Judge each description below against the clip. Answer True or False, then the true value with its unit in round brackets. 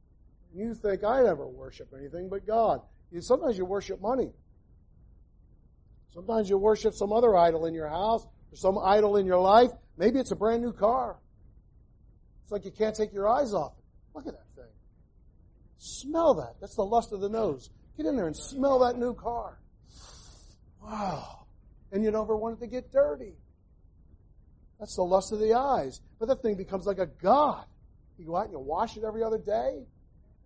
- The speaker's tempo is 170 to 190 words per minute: True (185 wpm)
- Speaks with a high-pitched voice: True (200 Hz)